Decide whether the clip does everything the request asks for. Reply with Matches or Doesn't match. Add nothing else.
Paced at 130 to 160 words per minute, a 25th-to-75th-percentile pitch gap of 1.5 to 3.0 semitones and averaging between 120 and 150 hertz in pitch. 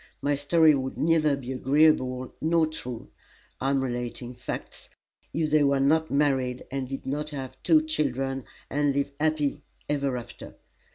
Matches